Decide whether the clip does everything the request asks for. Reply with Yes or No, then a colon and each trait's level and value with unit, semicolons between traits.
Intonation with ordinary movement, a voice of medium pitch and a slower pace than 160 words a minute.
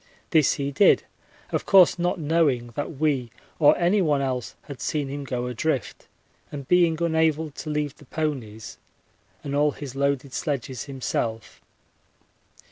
Yes: average, 3.2 semitones; medium, 145 Hz; average, 140 wpm